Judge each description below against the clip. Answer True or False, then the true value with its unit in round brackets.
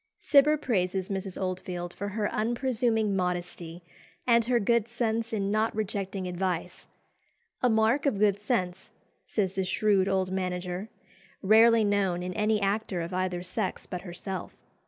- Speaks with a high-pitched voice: True (195 Hz)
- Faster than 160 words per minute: False (145 wpm)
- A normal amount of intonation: True (3.3 semitones)